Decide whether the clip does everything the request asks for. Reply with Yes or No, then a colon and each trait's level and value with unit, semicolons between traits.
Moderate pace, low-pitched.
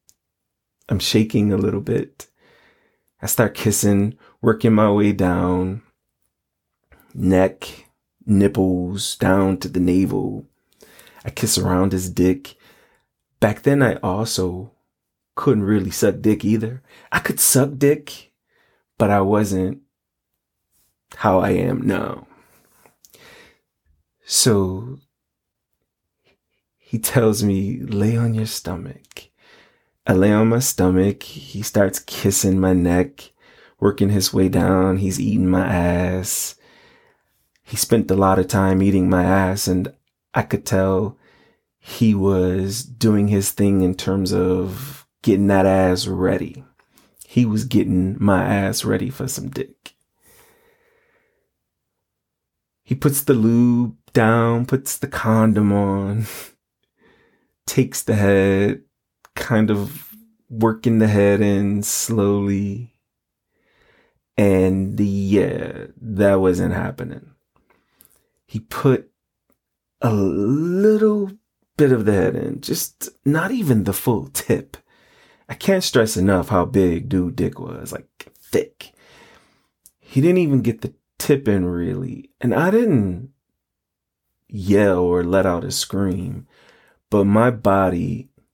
No: slow, 115 wpm; low, 100 Hz